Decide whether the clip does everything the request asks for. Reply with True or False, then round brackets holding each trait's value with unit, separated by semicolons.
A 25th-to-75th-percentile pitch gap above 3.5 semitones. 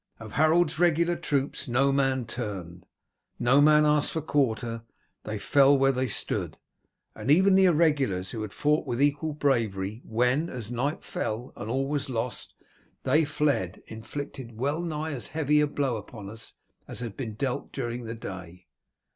True (4.8 semitones)